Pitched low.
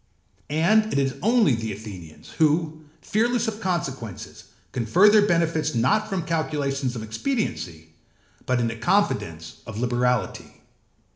No: medium, 145 Hz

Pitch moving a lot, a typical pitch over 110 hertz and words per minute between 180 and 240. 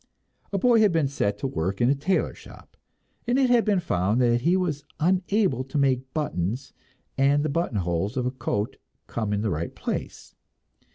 Yes: wide, 8.8 semitones; low, 135 Hz; average, 190 wpm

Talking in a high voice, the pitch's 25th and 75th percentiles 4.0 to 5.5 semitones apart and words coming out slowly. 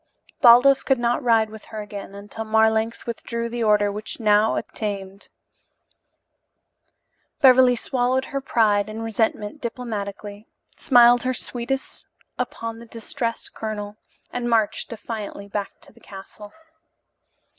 No: high, 225 Hz; narrow, 2.6 semitones; slow, 125 wpm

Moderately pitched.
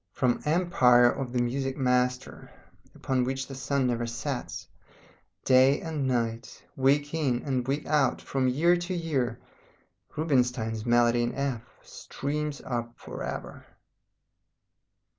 No: low, 130 Hz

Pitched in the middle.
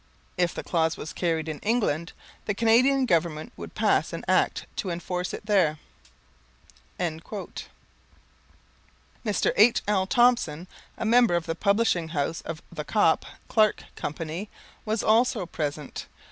Yes: medium, 180 Hz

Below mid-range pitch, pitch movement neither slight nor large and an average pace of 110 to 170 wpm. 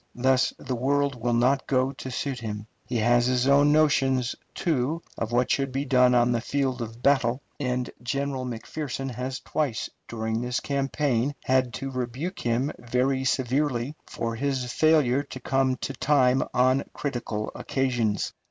No: low, 130 Hz; narrow, 2.2 semitones; average, 160 wpm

